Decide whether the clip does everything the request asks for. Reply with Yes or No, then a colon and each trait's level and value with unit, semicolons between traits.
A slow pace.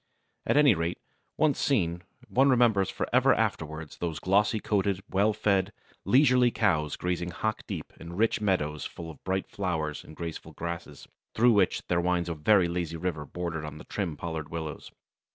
No: average, 170 wpm